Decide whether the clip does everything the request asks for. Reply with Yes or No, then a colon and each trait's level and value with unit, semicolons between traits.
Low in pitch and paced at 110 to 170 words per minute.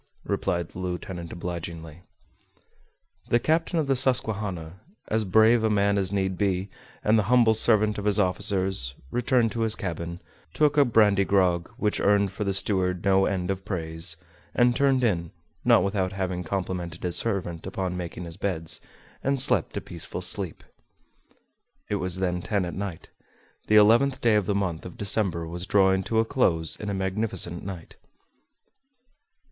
Yes: very low, 95 Hz; average, 165 wpm